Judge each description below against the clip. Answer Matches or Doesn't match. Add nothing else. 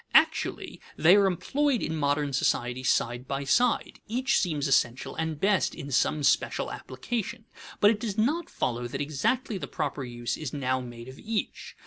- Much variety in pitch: Matches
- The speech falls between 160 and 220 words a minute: Matches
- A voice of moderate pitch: Matches